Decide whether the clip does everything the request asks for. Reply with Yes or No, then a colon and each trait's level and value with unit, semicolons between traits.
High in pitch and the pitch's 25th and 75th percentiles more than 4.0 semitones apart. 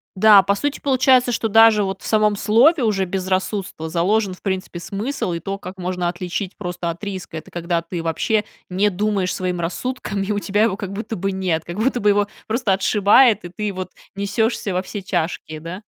No: high, 195 Hz; average, 2.9 semitones